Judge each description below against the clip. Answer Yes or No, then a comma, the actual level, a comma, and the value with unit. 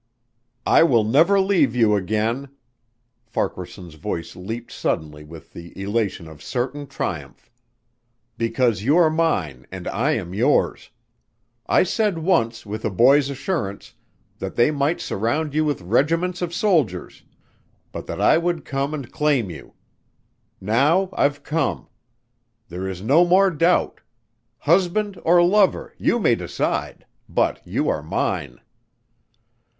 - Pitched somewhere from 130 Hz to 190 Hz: Yes, low, 135 Hz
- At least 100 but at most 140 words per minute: Yes, slow, 135 wpm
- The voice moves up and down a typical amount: No, wide, 8.6 semitones